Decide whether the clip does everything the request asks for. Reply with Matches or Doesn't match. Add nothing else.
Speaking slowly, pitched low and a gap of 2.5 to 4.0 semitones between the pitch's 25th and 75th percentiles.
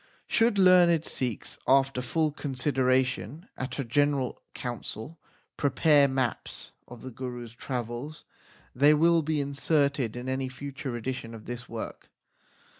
Matches